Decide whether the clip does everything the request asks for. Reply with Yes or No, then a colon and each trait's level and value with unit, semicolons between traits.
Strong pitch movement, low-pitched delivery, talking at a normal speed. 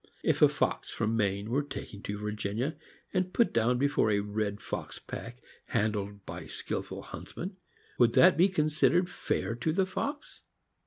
Yes: wide, 8.0 semitones; low, 120 Hz; average, 165 wpm